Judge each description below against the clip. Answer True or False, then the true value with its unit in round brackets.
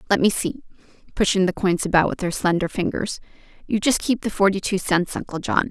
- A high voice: True (195 Hz)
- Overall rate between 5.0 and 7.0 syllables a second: True (5.8 syllables/s)